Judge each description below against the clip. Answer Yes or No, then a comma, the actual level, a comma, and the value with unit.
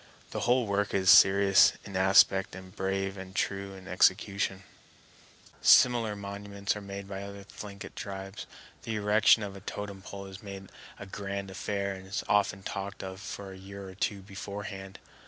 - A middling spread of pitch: No, narrow, 0.8 semitones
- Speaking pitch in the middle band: No, low, 100 Hz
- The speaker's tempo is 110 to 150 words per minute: No, average, 170 wpm